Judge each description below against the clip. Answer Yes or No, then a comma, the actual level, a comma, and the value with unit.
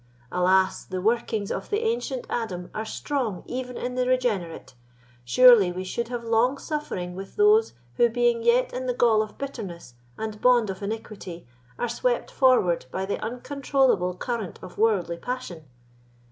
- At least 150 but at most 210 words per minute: Yes, average, 160 wpm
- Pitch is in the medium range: No, high, 230 Hz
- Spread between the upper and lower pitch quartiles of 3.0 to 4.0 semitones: No, average, 5.1 semitones